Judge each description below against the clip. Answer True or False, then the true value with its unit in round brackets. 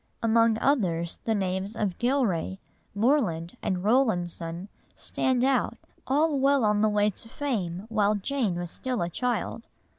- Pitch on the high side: True (215 Hz)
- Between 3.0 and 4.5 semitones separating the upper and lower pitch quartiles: False (5.6 semitones)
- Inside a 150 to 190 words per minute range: False (140 wpm)